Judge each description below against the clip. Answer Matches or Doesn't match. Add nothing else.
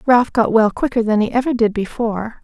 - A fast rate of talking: Matches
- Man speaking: Doesn't match